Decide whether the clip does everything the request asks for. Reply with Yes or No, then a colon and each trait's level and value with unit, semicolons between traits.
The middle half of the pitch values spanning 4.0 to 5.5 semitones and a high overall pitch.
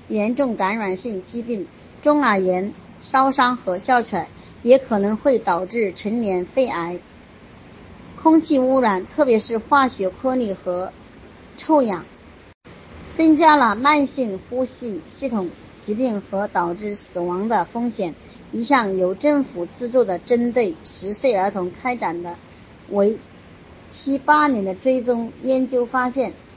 Yes: average, 5.2 semitones; high, 235 Hz